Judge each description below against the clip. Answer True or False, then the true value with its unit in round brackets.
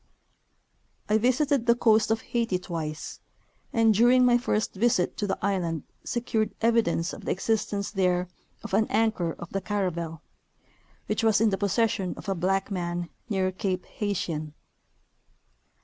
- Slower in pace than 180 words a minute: True (150 wpm)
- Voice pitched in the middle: False (200 Hz)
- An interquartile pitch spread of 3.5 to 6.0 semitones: True (3.9 semitones)